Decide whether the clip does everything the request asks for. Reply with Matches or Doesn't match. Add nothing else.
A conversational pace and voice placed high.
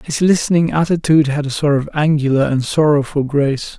Doesn't match